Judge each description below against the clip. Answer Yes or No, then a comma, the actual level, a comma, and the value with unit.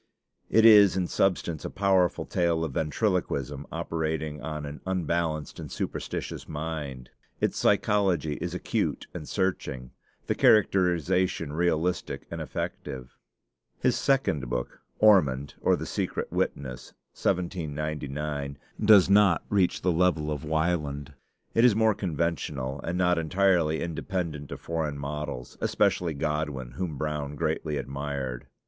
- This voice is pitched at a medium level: No, very low, 80 Hz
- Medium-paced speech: No, slow, 125 wpm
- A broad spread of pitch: No, average, 3.9 semitones